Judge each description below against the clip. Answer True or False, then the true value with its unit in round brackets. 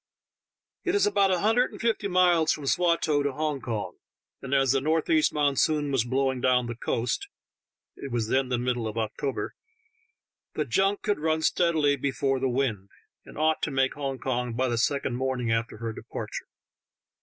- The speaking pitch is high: False (135 Hz)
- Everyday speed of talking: True (190 wpm)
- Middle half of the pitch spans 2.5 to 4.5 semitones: True (4.2 semitones)